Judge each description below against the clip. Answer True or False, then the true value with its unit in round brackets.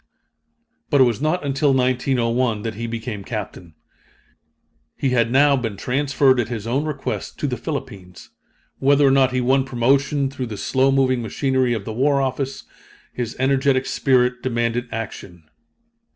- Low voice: True (130 Hz)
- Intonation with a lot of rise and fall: False (2.7 semitones)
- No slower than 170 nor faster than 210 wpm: False (155 wpm)